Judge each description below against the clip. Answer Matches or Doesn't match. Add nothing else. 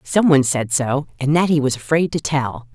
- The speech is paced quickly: Matches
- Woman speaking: Matches